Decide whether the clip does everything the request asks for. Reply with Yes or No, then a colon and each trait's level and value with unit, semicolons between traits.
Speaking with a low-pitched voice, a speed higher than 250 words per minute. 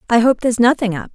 No: high, 230 Hz; fast, 265 wpm